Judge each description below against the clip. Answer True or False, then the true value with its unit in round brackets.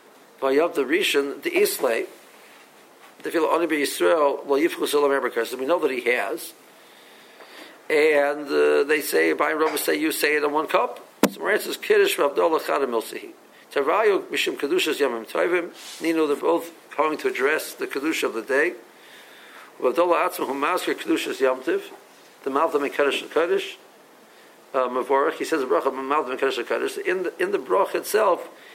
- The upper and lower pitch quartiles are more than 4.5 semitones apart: False (4.2 semitones)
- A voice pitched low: False (390 Hz)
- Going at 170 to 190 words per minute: True (175 wpm)